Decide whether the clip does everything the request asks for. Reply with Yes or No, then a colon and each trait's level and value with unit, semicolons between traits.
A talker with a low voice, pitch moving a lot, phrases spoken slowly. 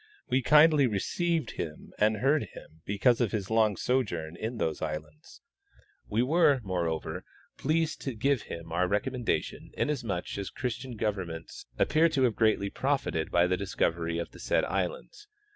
No: low, 110 Hz; wide, 7.1 semitones; average, 160 wpm